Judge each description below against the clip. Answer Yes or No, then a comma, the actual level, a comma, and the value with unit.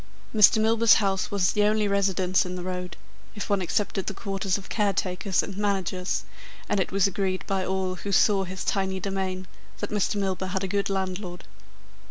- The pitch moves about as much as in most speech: No, narrow, 1.4 semitones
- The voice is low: No, high, 195 Hz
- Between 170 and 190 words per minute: Yes, average, 185 wpm